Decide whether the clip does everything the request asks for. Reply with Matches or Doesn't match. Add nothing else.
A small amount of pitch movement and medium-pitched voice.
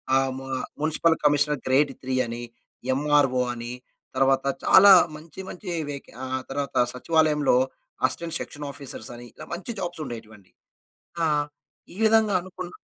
Doesn't match